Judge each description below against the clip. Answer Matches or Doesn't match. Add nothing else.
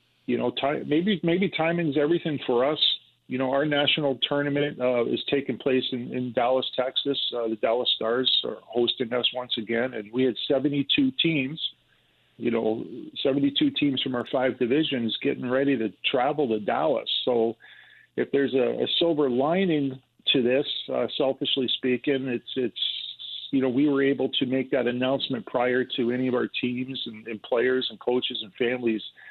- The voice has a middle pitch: Doesn't match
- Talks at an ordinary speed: Matches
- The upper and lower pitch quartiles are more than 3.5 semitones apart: Doesn't match